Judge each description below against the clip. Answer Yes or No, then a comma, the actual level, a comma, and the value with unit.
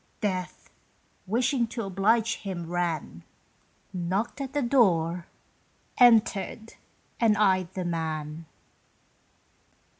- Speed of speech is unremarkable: No, slow, 90 wpm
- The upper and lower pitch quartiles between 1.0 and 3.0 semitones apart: No, average, 5.0 semitones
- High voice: Yes, high, 195 Hz